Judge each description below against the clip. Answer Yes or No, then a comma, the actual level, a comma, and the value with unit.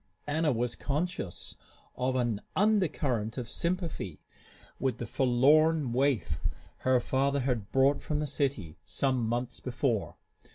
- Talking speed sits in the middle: No, slow, 125 wpm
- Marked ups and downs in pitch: No, average, 3.6 semitones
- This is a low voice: Yes, low, 130 Hz